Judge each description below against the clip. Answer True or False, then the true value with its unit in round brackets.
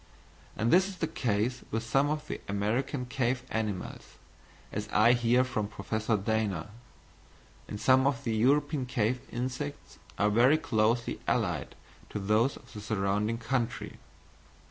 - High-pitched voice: False (115 Hz)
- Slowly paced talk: False (145 wpm)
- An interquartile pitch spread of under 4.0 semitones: True (3.4 semitones)